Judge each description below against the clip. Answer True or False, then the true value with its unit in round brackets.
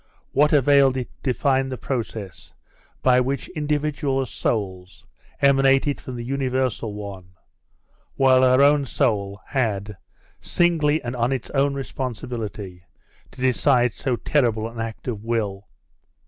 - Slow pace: True (130 wpm)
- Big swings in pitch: False (3.8 semitones)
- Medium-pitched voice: False (130 Hz)